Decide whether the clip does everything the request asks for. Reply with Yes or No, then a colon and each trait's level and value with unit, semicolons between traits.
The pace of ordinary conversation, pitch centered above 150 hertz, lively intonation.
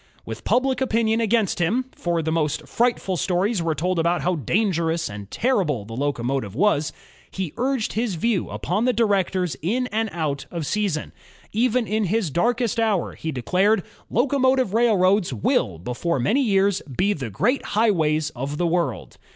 Yes: average, 175 wpm; medium, 185 Hz; wide, 6.4 semitones